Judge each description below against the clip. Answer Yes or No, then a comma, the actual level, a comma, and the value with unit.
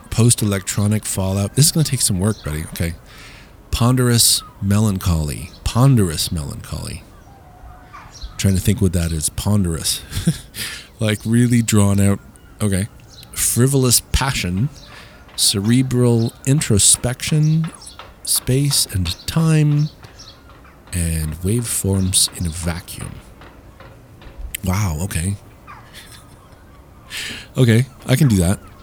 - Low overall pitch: Yes, low, 105 Hz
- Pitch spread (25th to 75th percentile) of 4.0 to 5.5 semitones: Yes, average, 4.7 semitones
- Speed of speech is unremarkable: No, slow, 100 wpm